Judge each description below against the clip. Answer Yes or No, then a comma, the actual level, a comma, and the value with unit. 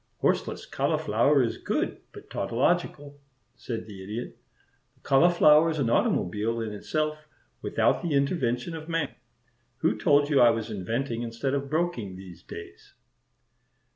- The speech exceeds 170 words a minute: No, average, 140 wpm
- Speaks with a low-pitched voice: Yes, low, 130 Hz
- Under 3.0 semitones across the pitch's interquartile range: No, average, 5.1 semitones